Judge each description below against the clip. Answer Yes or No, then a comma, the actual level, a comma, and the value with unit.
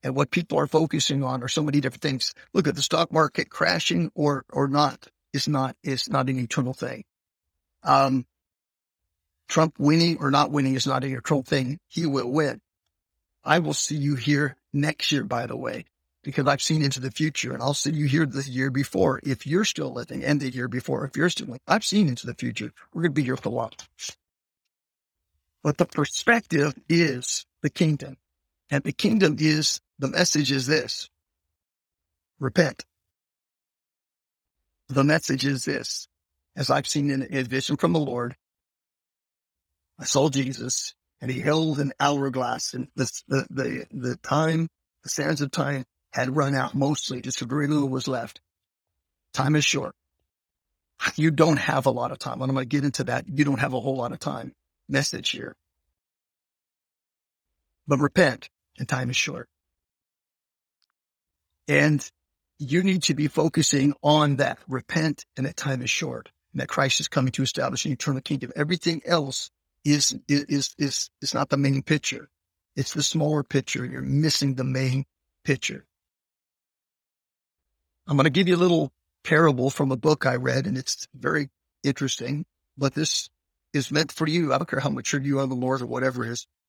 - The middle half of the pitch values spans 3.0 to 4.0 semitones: Yes, average, 3.5 semitones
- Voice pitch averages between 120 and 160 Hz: Yes, low, 135 Hz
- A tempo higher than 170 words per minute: Yes, average, 180 wpm